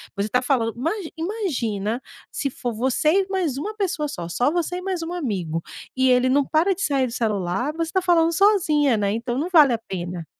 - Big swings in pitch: Yes, wide, 6.8 semitones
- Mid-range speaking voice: No, very high, 275 Hz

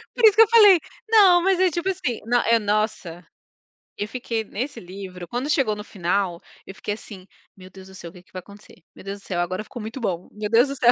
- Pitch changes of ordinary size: No, wide, 6.0 semitones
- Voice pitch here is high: Yes, high, 215 Hz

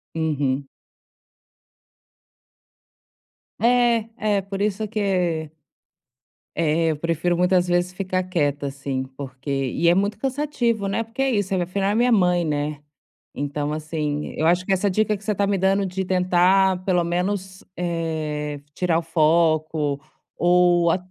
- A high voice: No, medium, 180 Hz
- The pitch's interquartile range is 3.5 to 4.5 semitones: Yes, average, 4.0 semitones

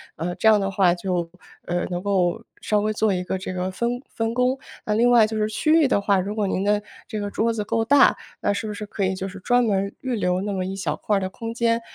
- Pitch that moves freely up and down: No, average, 3.2 semitones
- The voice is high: Yes, high, 205 Hz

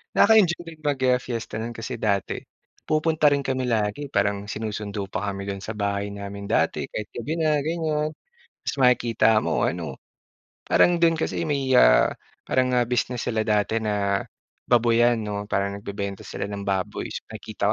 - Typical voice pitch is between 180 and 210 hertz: No, low, 110 Hz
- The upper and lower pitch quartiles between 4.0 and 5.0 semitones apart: Yes, average, 4.6 semitones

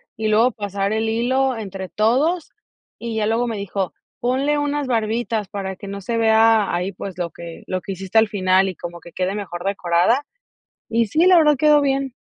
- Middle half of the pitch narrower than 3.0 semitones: No, average, 4.1 semitones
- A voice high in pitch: Yes, high, 220 Hz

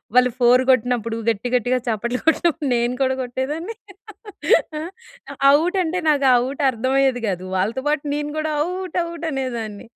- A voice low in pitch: No, very high, 260 Hz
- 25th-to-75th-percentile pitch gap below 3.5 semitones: No, average, 4.3 semitones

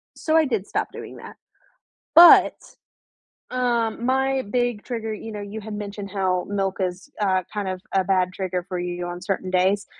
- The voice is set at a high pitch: Yes, high, 200 Hz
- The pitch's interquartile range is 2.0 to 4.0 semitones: Yes, average, 3.6 semitones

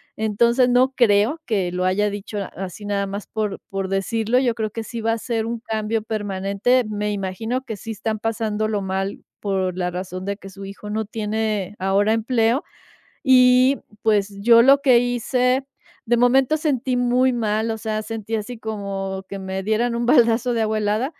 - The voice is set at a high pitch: Yes, high, 220 Hz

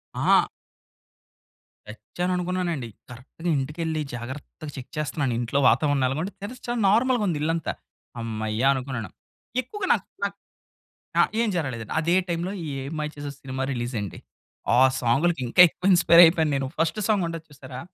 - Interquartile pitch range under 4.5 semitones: No, average, 5.2 semitones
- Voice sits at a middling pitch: Yes, medium, 150 Hz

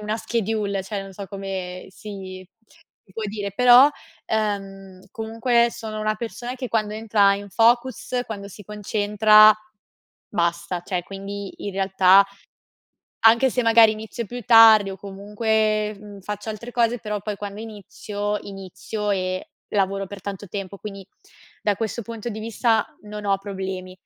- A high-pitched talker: Yes, high, 210 Hz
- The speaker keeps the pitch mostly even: Yes, narrow, 2.1 semitones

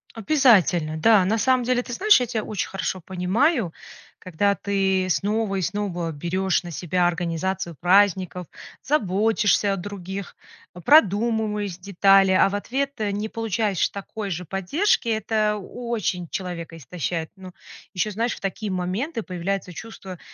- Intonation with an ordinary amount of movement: Yes, average, 3.5 semitones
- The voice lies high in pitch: Yes, high, 195 Hz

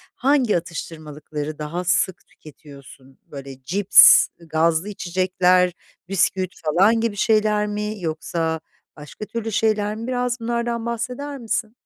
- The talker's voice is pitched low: No, high, 190 Hz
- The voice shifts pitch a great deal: Yes, wide, 5.9 semitones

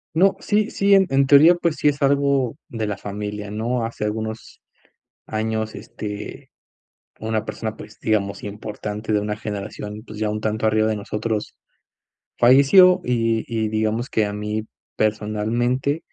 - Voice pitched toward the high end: No, low, 110 Hz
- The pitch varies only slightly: No, average, 3.4 semitones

